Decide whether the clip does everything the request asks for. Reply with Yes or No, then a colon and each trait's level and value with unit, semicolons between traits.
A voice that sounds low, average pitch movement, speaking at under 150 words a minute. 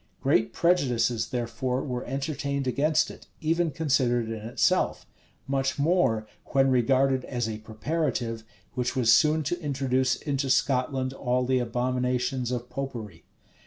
No: low, 130 Hz; narrow, 2.3 semitones; slow, 135 wpm